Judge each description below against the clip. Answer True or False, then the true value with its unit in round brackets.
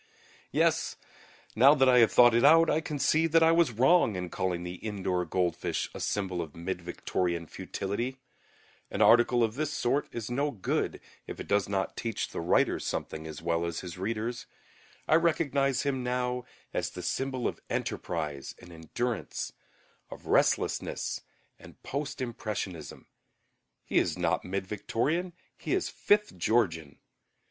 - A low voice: True (115 Hz)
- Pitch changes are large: True (6.9 semitones)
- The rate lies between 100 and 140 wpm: False (155 wpm)